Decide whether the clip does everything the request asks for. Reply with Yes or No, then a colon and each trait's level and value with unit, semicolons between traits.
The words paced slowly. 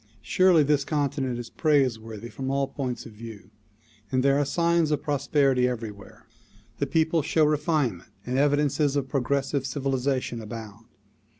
No: average, 145 wpm